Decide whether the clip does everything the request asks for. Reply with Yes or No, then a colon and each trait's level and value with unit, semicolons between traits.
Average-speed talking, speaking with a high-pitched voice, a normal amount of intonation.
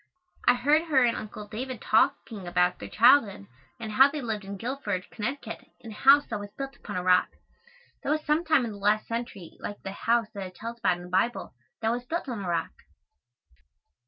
No: fast, 215 wpm; high, 225 Hz; average, 4.7 semitones